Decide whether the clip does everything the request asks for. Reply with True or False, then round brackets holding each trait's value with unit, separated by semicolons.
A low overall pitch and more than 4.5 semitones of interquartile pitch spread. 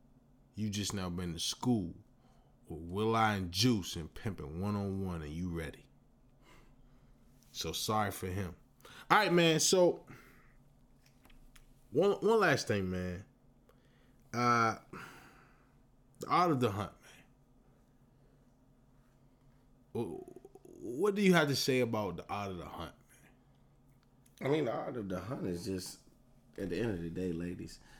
True (125 Hz; 5.5 semitones)